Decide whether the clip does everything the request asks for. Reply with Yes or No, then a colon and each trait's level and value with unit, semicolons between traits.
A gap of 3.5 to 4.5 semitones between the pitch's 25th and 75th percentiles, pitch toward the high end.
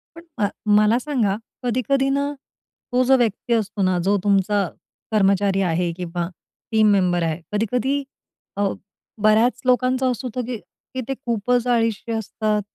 Yes: average, 4.0 semitones; high, 220 Hz